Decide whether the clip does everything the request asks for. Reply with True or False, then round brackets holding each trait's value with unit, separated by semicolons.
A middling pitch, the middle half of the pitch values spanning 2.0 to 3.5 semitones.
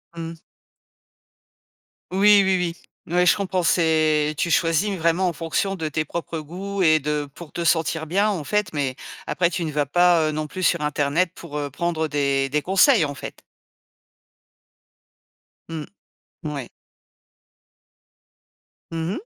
True (165 Hz; 3.1 semitones)